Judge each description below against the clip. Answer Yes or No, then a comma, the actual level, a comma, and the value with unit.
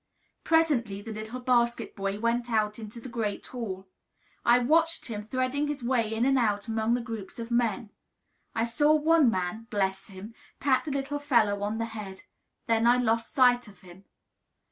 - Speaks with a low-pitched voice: No, high, 230 Hz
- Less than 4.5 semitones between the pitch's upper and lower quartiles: Yes, average, 3.1 semitones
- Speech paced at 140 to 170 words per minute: No, average, 180 wpm